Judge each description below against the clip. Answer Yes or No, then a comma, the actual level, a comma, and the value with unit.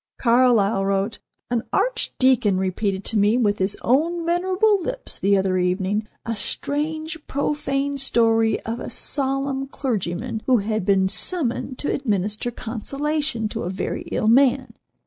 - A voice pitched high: Yes, high, 235 Hz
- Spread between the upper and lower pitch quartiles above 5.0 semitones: Yes, wide, 5.5 semitones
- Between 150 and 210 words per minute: No, average, 140 wpm